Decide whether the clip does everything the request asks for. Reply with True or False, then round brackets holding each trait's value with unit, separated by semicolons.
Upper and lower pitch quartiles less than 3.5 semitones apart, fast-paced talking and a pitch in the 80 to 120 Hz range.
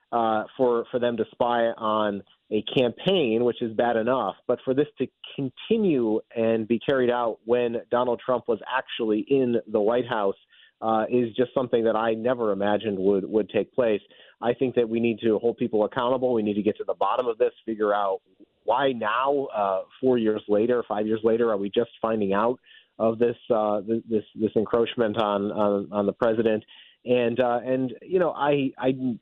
False (2.5 semitones; 195 wpm; 115 Hz)